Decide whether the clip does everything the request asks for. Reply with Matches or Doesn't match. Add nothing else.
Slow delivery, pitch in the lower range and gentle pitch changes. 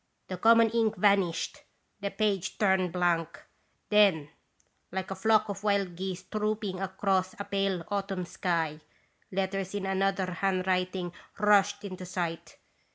Doesn't match